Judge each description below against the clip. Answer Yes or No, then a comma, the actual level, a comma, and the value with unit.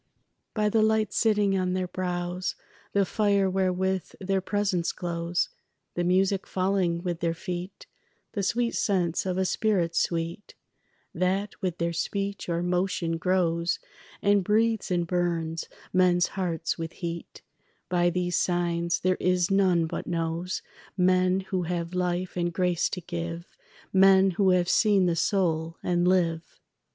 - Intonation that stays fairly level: Yes, narrow, 2.0 semitones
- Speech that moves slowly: No, average, 145 wpm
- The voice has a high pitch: No, medium, 180 Hz